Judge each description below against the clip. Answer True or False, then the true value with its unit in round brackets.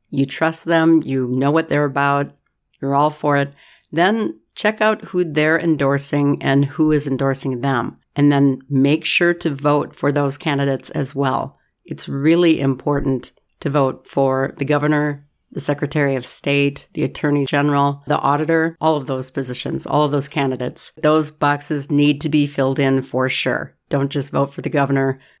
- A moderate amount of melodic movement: False (1.8 semitones)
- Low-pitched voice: False (145 Hz)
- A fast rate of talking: False (175 wpm)